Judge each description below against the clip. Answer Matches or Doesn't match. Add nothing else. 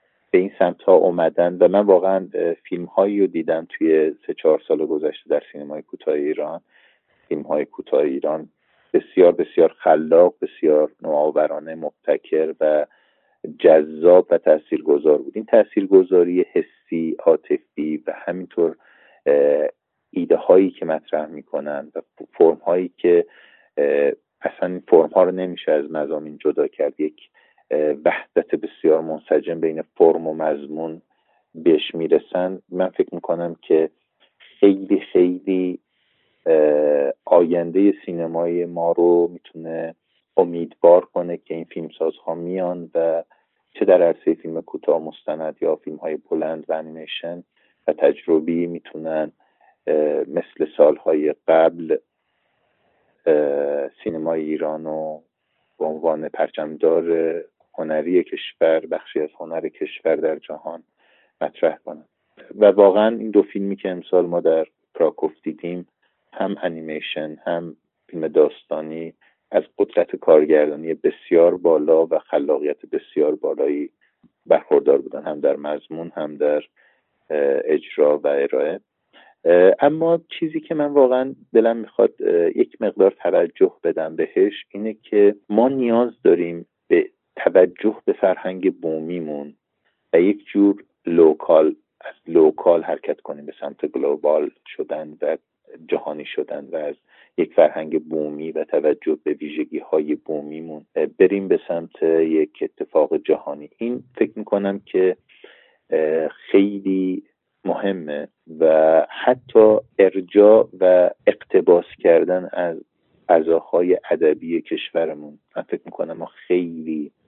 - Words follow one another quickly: Doesn't match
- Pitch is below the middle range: Doesn't match